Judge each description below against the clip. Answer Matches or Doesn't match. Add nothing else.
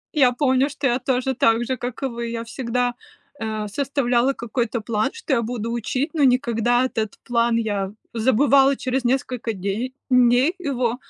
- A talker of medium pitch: Doesn't match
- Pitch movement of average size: Doesn't match